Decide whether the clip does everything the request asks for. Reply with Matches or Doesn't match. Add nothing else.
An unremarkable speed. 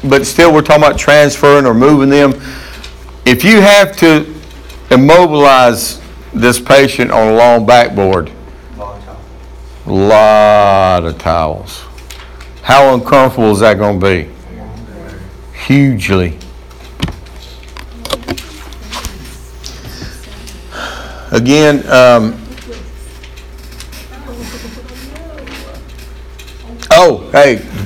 Doesn't match